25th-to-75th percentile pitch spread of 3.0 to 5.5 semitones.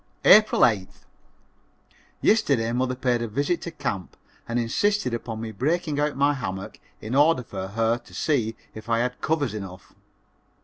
Yes: average, 4.5 semitones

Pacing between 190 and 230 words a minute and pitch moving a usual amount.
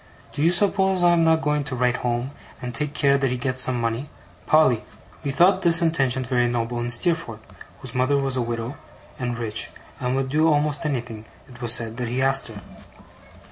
Yes: fast, 205 wpm; average, 3.7 semitones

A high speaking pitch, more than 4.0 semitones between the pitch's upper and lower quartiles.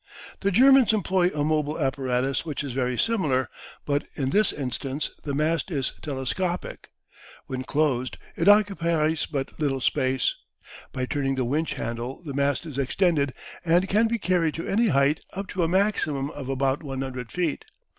No: medium, 150 Hz; average, 4.8 semitones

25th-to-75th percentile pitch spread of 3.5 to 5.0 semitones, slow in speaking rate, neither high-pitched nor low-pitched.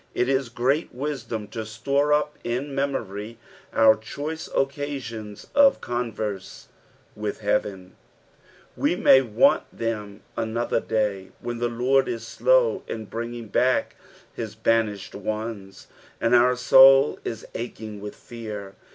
No: average, 3.9 semitones; slow, 125 wpm; low, 115 Hz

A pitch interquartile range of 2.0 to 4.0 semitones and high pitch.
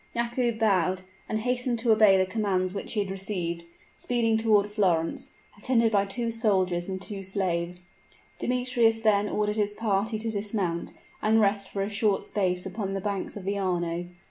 Yes: average, 2.9 semitones; high, 205 Hz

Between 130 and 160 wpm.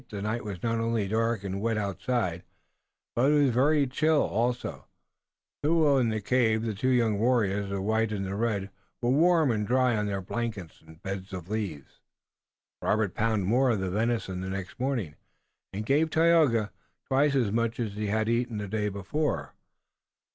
No: average, 180 wpm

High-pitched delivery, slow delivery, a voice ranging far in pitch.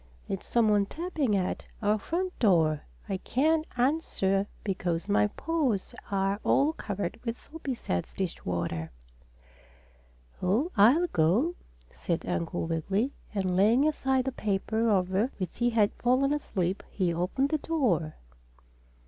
Yes: high, 210 Hz; slow, 130 wpm; wide, 6.5 semitones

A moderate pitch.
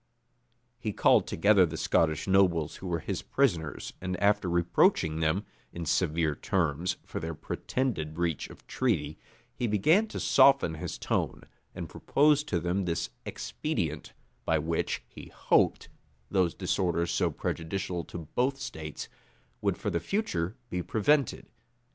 No: very low, 85 Hz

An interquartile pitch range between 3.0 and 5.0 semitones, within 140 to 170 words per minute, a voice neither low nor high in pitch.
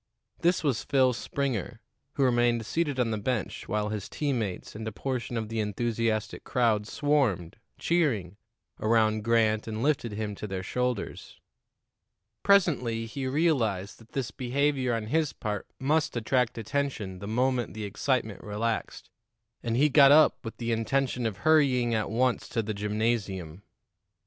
No: average, 3.7 semitones; average, 155 wpm; low, 115 Hz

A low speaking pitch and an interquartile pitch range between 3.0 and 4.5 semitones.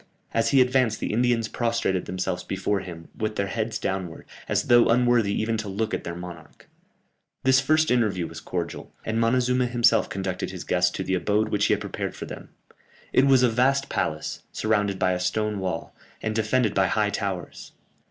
Yes: low, 110 Hz; average, 4.2 semitones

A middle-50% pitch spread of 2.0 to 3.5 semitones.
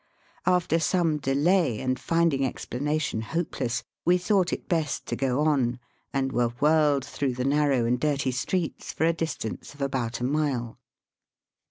No: average, 4.0 semitones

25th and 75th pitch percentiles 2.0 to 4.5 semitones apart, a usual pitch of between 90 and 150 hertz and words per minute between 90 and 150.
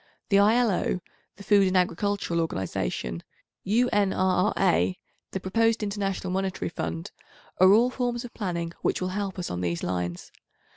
No: average, 3.4 semitones; high, 190 Hz; average, 140 wpm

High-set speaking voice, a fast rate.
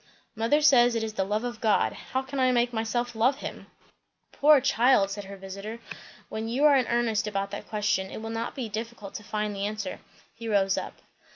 Yes: high, 225 Hz; fast, 210 wpm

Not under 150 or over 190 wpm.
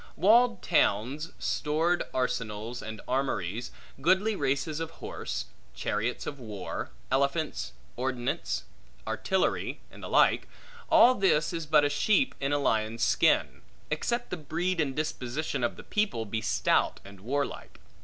No: slow, 135 wpm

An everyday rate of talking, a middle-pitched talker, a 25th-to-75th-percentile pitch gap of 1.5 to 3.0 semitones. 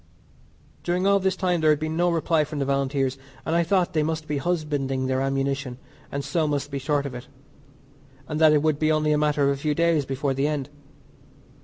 No: fast, 220 wpm; medium, 150 Hz; narrow, 2.6 semitones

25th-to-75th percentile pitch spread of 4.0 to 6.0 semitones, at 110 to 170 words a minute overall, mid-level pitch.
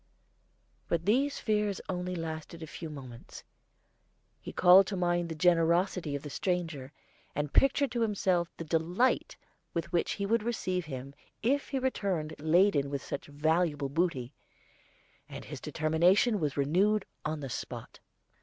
Yes: average, 4.4 semitones; average, 145 wpm; medium, 170 Hz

